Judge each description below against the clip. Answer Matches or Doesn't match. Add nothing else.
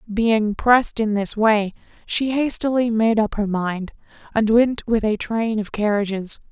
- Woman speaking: Matches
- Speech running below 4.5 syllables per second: Matches